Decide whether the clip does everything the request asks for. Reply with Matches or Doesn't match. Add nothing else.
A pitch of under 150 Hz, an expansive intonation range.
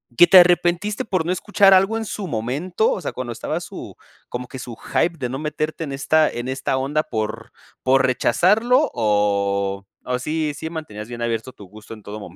Matches